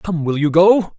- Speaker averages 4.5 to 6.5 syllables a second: No, 4.3 syllables/s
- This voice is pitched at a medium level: Yes, medium, 170 Hz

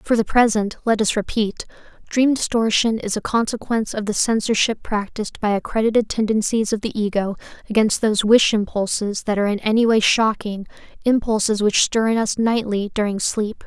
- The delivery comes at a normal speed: Yes, average, 170 wpm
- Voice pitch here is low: No, high, 215 Hz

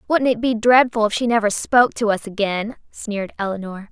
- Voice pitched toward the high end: Yes, high, 220 Hz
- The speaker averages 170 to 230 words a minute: Yes, average, 200 wpm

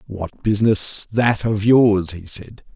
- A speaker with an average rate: Yes, average, 150 wpm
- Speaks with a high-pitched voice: No, low, 105 Hz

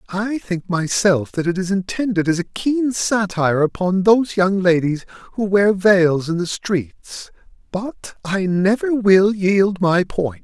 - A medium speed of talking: Yes, average, 160 wpm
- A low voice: No, high, 190 Hz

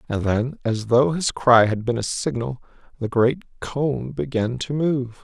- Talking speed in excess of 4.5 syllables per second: No, 3.9 syllables/s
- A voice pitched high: No, low, 125 Hz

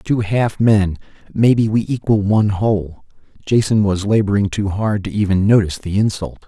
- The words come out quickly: No, average, 160 wpm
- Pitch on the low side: Yes, low, 105 Hz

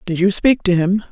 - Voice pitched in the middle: No, high, 195 Hz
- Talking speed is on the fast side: Yes, fast, 270 wpm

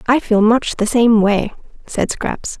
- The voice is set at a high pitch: Yes, high, 225 Hz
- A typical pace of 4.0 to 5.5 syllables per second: No, 3.8 syllables/s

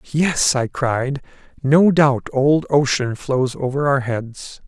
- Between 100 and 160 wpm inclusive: Yes, average, 140 wpm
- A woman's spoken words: No, male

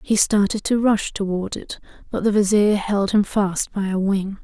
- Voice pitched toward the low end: No, high, 200 Hz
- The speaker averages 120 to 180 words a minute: No, fast, 205 wpm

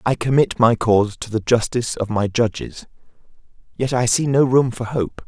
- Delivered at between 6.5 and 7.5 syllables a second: No, 5.1 syllables/s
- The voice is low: Yes, low, 120 Hz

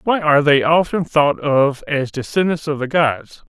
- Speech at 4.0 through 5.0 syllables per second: Yes, 4.5 syllables/s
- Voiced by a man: Yes, male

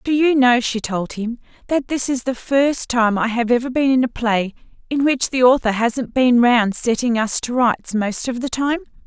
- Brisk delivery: Yes, fast, 225 wpm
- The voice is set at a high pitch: Yes, high, 245 Hz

